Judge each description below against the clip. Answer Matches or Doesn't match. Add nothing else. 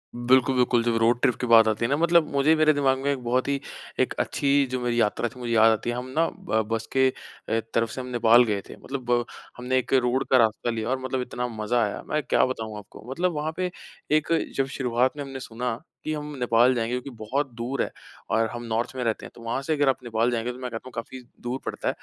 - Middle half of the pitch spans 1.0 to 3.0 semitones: Matches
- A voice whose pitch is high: Doesn't match